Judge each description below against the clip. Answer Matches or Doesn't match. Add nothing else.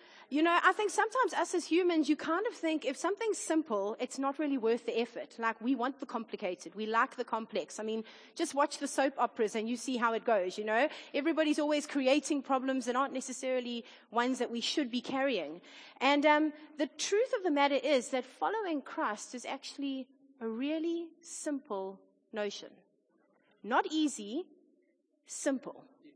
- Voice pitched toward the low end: Doesn't match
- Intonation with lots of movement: Doesn't match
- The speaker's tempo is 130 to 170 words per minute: Doesn't match